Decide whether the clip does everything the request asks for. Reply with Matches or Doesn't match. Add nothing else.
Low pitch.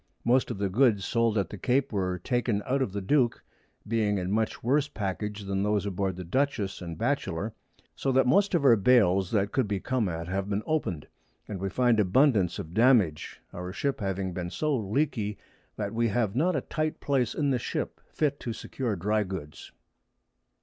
Matches